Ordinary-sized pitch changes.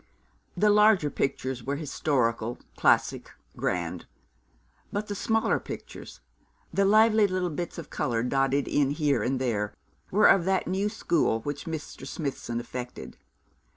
No: wide, 7.1 semitones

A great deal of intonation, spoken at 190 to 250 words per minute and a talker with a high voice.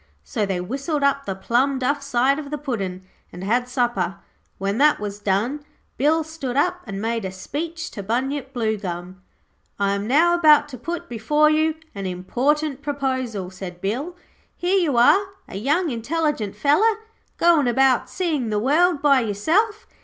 No: wide, 6.5 semitones; average, 165 wpm; very high, 260 Hz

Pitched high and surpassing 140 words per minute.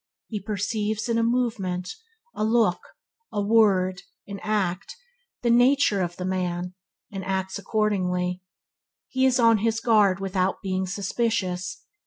No: high, 200 Hz; slow, 135 wpm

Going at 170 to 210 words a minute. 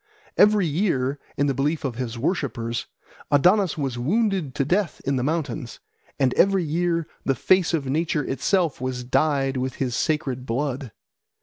No: average, 160 wpm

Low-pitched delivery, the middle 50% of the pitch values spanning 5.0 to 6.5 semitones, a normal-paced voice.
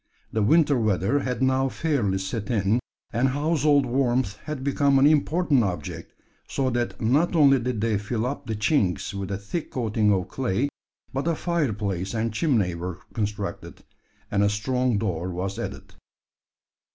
Yes: low, 120 Hz; wide, 5.4 semitones; average, 160 wpm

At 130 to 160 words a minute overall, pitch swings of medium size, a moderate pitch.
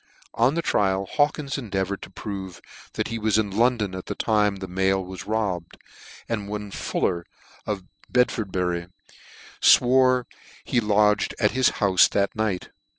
No: average, 155 wpm; average, 3.3 semitones; low, 105 Hz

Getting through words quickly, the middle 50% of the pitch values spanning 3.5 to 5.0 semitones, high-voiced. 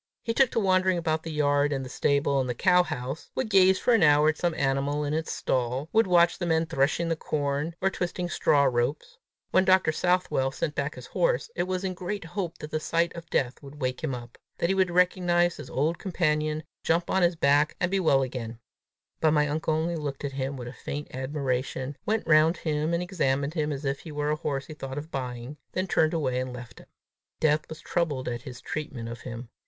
No: fast, 230 wpm; average, 4.1 semitones; medium, 155 Hz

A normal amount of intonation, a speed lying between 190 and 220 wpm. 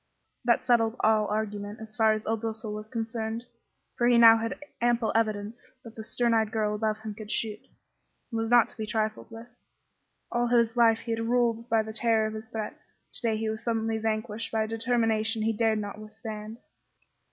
No: narrow, 1.0 semitones; average, 200 wpm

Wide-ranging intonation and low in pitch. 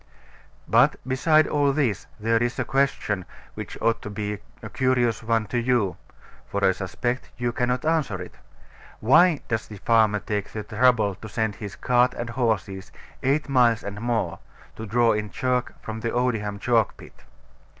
No: average, 3.1 semitones; low, 115 Hz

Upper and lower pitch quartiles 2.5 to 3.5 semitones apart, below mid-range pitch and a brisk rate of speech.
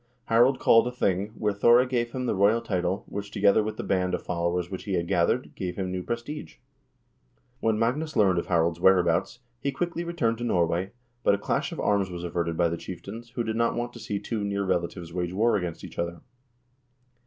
No: average, 4.9 semitones; low, 100 Hz; fast, 215 wpm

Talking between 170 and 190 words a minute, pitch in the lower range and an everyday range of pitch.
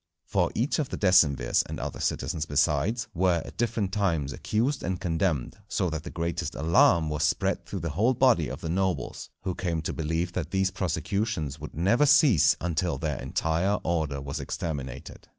Yes: average, 180 wpm; very low, 85 Hz; average, 4.0 semitones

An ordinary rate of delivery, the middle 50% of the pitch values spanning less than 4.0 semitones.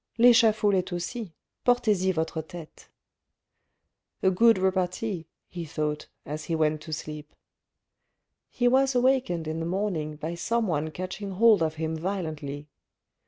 No: average, 145 wpm; average, 5.2 semitones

